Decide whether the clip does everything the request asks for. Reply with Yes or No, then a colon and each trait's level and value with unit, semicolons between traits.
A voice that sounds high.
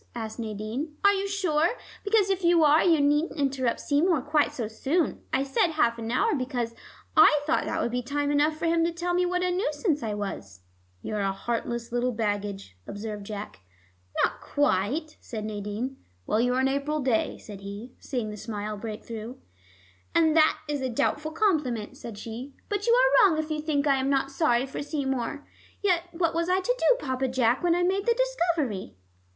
Yes: very high, 275 Hz